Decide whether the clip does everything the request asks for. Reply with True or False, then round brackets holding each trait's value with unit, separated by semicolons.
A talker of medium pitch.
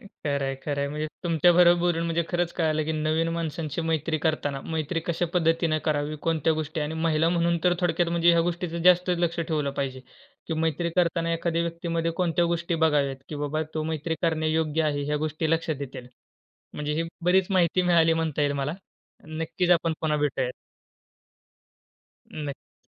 True (160 Hz)